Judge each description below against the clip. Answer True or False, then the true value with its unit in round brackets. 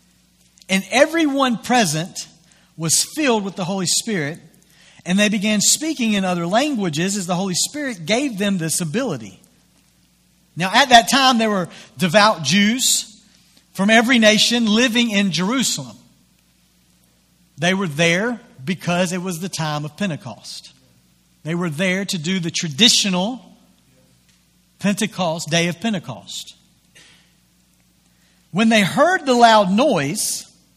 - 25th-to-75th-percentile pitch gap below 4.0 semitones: False (5.3 semitones)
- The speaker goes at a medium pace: False (125 wpm)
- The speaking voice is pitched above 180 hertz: True (190 Hz)